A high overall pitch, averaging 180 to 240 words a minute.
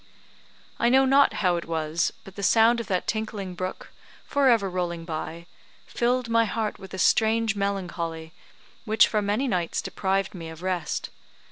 No: high, 195 Hz; average, 165 wpm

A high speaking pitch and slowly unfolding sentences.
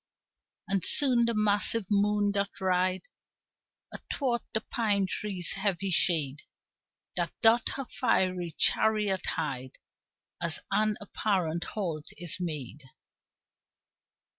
Yes: high, 195 Hz; slow, 105 wpm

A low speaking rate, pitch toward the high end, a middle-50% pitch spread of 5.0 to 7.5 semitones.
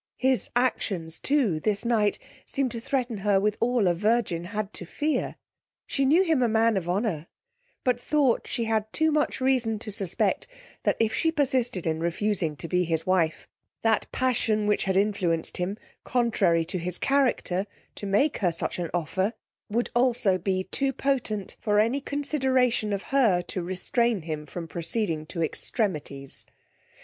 No: average, 165 wpm; high, 210 Hz; wide, 5.6 semitones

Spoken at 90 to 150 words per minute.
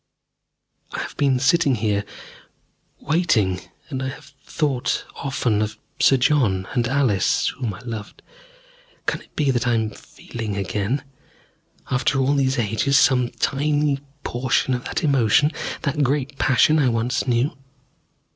Yes: average, 140 wpm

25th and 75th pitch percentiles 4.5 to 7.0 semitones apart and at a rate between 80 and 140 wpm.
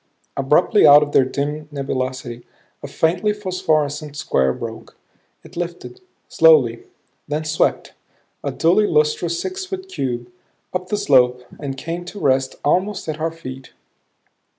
Yes: average, 5.1 semitones; slow, 135 wpm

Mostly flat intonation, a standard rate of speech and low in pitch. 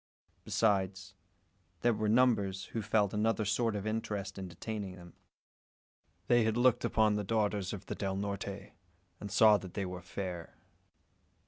Yes: narrow, 2.3 semitones; average, 150 wpm; low, 100 Hz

